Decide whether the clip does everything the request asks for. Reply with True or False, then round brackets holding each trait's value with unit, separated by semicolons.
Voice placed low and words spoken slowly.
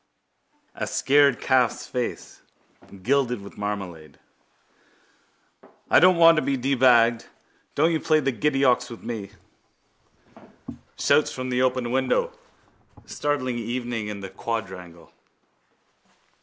True (125 Hz; 115 wpm)